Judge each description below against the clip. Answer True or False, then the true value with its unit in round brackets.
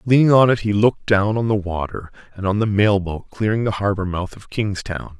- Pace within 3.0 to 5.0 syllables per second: False (5.4 syllables/s)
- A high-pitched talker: False (100 Hz)